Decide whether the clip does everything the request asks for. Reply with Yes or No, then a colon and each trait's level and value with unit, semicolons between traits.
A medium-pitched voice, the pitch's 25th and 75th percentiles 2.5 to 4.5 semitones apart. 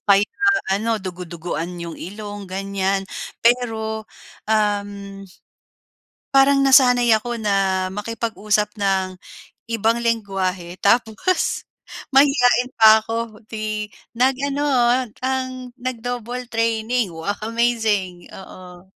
No: high, 220 Hz; average, 3.7 semitones